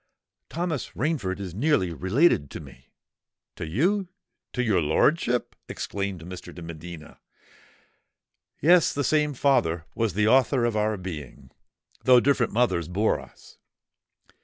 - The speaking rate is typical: No, slow, 120 wpm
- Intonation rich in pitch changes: Yes, wide, 8.1 semitones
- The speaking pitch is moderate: No, low, 110 Hz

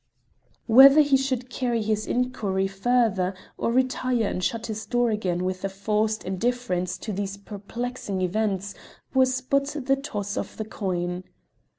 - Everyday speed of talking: Yes, average, 150 wpm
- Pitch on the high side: Yes, high, 220 Hz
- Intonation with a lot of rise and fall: No, average, 4.3 semitones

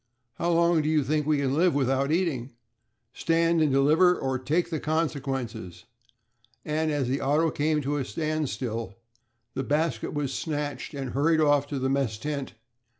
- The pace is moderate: Yes, average, 165 wpm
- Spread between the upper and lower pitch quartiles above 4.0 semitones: No, average, 2.8 semitones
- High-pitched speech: No, medium, 145 Hz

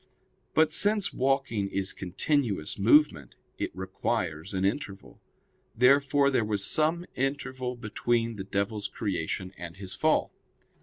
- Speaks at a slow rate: Yes, slow, 120 wpm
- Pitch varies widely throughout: Yes, wide, 6.1 semitones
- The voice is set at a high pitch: No, low, 110 Hz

